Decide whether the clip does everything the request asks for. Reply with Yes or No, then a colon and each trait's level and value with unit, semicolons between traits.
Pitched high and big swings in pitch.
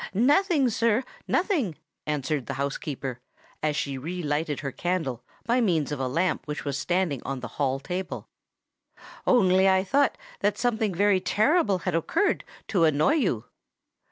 No: medium, 180 Hz; wide, 7.4 semitones